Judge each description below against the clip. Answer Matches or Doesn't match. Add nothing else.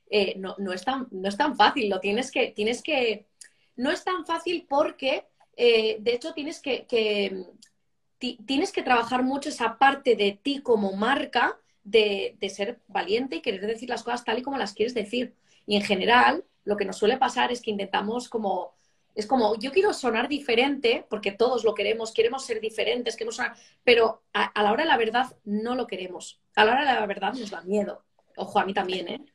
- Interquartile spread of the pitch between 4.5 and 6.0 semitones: Matches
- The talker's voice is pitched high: Matches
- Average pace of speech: Doesn't match